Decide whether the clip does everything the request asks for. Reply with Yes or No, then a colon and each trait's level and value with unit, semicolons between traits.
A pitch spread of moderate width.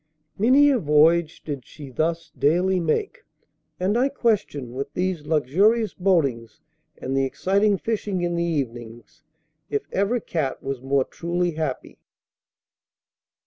No: wide, 5.9 semitones